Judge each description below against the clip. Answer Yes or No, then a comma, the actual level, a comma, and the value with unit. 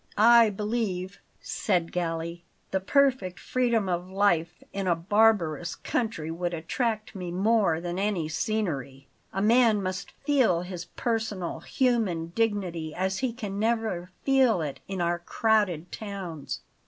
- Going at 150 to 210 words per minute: No, slow, 135 wpm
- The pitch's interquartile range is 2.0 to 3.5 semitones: No, average, 4.3 semitones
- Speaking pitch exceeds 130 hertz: Yes, high, 190 Hz